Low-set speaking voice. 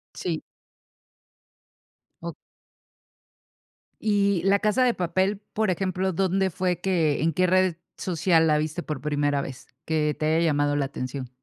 No: medium, 170 Hz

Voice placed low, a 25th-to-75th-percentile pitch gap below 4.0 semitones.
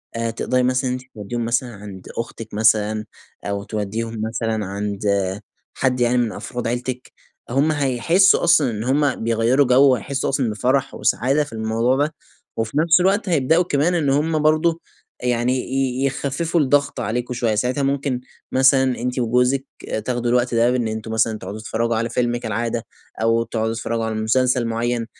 Yes: low, 125 Hz; average, 3.1 semitones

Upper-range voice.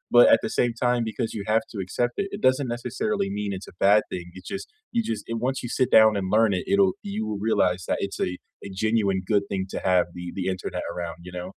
No: low, 110 Hz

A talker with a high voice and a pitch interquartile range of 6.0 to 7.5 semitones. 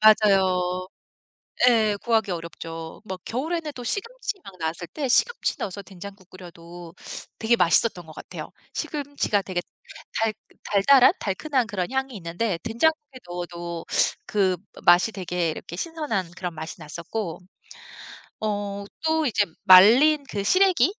Yes: high, 200 Hz; wide, 6.5 semitones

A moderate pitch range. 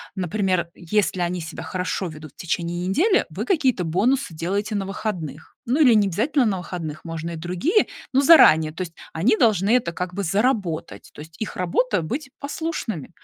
No: wide, 5.8 semitones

